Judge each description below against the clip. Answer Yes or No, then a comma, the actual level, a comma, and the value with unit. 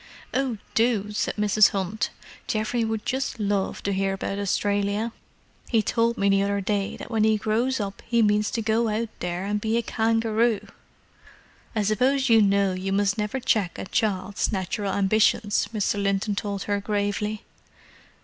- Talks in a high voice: Yes, high, 210 Hz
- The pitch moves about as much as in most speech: No, narrow, 2.0 semitones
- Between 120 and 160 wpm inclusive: No, average, 170 wpm